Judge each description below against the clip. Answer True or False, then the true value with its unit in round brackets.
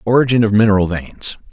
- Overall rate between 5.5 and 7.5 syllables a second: True (6.2 syllables/s)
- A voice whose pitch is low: True (110 Hz)